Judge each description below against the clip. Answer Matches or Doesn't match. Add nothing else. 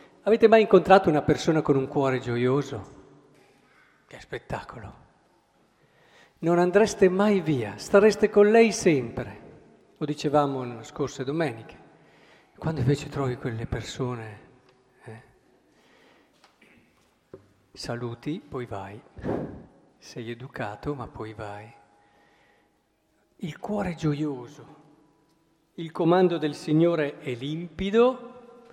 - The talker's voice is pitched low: Doesn't match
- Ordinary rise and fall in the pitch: Doesn't match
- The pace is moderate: Doesn't match